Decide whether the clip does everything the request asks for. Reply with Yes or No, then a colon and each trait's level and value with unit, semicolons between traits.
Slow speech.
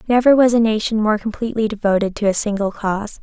No: fast, 205 wpm